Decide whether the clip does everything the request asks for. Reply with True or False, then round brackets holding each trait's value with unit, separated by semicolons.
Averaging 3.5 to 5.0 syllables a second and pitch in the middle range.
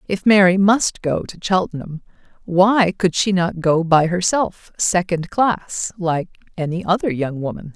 True (4.2 syllables/s; 180 Hz)